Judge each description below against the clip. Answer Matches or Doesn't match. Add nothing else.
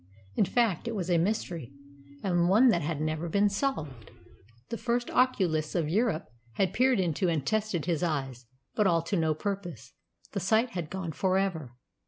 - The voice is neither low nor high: Matches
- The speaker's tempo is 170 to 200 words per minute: Matches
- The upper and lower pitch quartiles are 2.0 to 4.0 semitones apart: Doesn't match